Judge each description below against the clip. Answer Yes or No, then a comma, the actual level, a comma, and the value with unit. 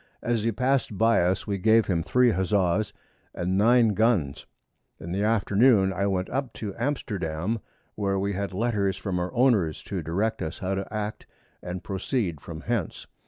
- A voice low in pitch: Yes, low, 100 Hz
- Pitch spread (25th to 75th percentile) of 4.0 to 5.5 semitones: No, average, 3.6 semitones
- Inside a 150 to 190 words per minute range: Yes, average, 170 wpm